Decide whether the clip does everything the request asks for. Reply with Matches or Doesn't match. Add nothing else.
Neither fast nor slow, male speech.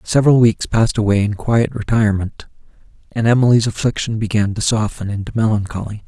Matches